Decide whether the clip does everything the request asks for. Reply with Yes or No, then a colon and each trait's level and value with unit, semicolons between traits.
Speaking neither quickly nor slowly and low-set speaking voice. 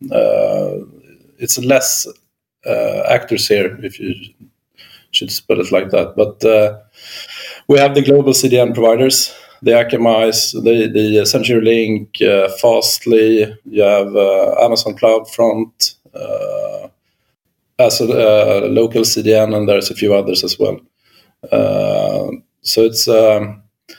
No: slow, 130 wpm; low, 115 Hz